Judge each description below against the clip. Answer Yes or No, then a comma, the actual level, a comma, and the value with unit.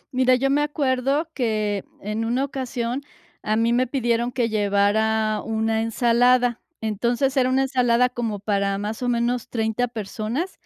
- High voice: Yes, high, 235 Hz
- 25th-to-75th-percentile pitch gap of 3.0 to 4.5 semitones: No, narrow, 2.6 semitones